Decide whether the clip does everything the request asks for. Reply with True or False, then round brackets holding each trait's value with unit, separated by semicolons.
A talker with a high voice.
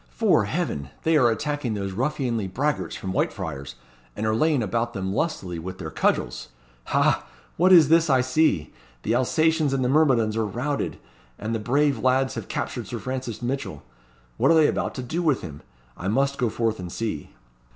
False (120 Hz)